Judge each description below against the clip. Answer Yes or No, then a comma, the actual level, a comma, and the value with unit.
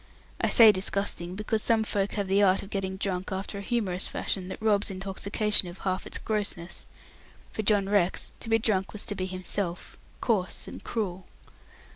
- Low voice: No, high, 195 Hz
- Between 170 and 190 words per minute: Yes, average, 180 wpm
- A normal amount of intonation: No, narrow, 2.1 semitones